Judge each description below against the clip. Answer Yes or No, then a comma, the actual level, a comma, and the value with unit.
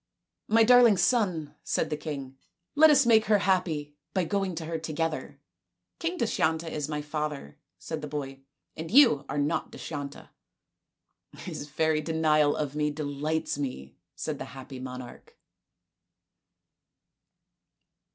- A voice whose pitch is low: No, medium, 155 Hz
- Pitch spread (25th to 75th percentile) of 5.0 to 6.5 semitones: No, average, 3.9 semitones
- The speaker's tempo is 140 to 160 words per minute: Yes, average, 150 wpm